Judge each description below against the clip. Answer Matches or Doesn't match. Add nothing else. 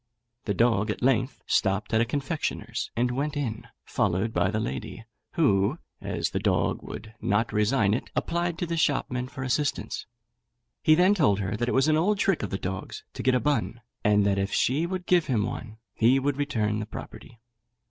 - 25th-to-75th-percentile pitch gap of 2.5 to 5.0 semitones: Doesn't match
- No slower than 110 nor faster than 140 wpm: Doesn't match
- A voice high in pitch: Doesn't match